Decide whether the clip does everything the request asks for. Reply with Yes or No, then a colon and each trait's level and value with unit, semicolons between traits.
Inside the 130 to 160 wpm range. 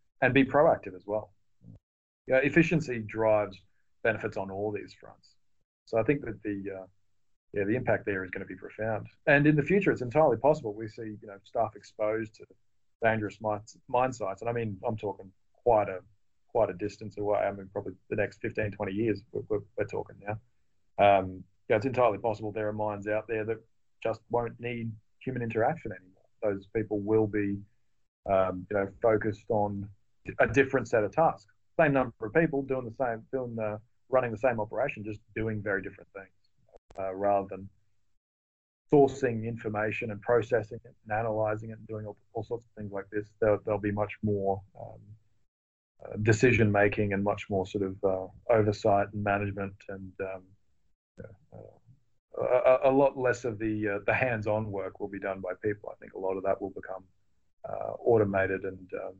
No: average, 190 wpm